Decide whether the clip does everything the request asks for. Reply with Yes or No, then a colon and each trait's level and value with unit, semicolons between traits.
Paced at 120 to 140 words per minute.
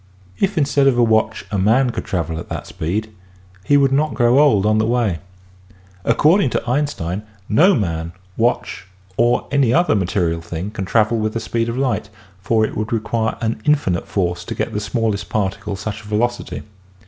No: average, 185 wpm